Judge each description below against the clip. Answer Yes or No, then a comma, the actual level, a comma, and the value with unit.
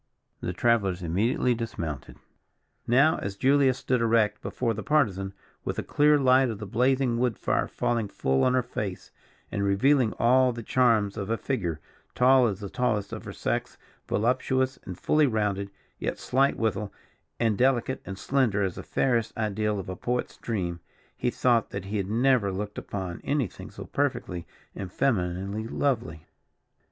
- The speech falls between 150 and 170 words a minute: Yes, average, 165 wpm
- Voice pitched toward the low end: Yes, low, 115 Hz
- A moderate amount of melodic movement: Yes, average, 4.5 semitones